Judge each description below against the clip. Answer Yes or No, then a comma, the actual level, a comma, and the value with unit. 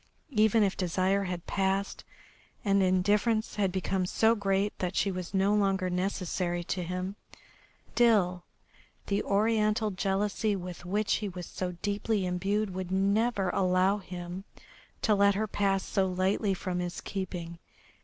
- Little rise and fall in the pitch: Yes, narrow, 2.0 semitones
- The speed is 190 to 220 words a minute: No, average, 145 wpm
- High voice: Yes, high, 195 Hz